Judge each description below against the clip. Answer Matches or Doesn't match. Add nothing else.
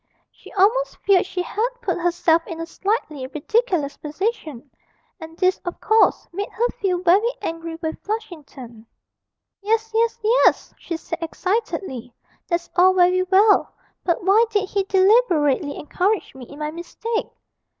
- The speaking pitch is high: Matches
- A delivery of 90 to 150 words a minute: Matches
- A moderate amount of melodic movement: Matches